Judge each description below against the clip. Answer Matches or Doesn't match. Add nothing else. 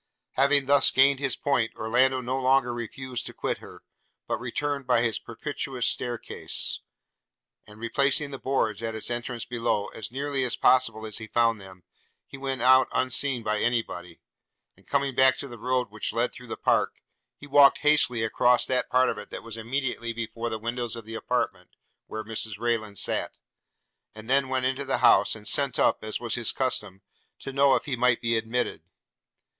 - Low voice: Matches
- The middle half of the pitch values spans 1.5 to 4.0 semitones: Matches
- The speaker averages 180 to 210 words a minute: Matches